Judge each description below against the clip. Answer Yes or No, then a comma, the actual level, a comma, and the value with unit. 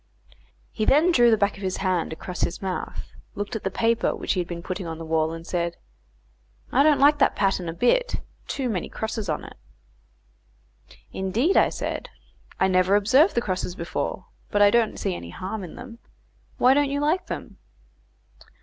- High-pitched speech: Yes, high, 200 Hz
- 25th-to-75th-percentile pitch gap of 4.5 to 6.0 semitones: Yes, wide, 5.5 semitones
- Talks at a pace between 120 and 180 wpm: No, average, 190 wpm